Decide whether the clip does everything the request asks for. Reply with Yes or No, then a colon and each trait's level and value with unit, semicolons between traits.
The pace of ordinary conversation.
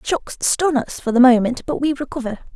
No: fast, 210 wpm